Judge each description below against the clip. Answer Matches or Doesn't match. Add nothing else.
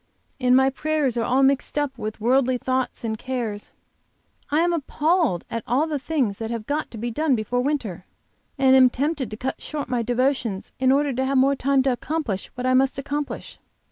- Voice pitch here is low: Doesn't match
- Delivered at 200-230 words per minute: Matches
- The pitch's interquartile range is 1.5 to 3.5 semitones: Matches